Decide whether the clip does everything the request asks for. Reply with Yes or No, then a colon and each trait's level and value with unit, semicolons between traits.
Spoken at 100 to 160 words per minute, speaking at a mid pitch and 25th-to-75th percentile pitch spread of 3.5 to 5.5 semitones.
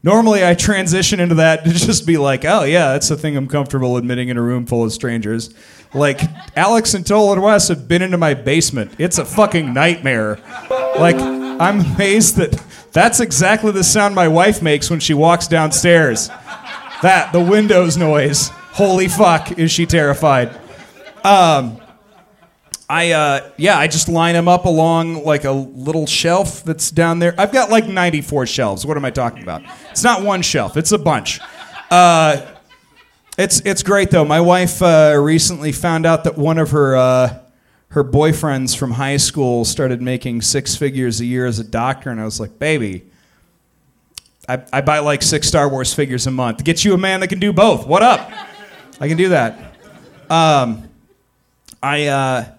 No: average, 180 wpm; medium, 155 Hz; average, 4.7 semitones